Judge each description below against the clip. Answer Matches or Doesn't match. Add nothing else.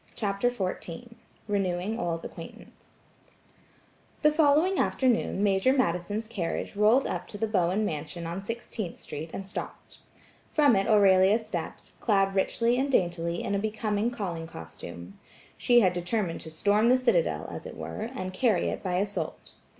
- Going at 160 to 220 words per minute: Doesn't match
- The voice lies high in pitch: Matches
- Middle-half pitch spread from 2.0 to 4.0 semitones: Doesn't match